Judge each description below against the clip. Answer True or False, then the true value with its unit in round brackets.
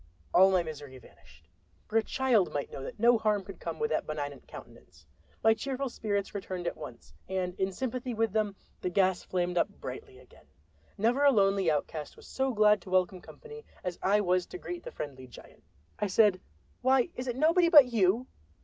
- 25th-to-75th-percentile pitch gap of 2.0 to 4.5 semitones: False (5.6 semitones)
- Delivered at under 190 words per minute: False (195 wpm)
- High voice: True (195 Hz)